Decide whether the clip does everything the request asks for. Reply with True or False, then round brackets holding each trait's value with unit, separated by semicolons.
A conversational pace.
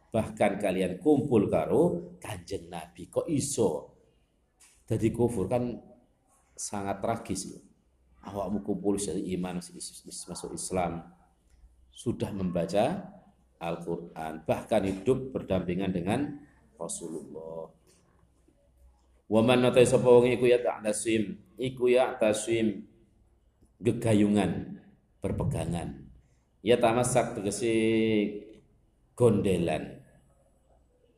False (75 wpm)